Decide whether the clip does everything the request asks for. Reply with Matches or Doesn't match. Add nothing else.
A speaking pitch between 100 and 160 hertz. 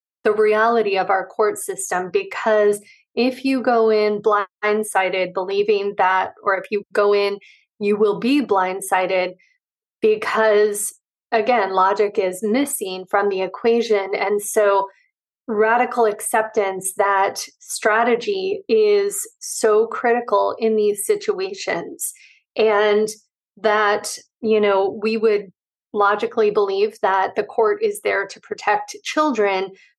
Doesn't match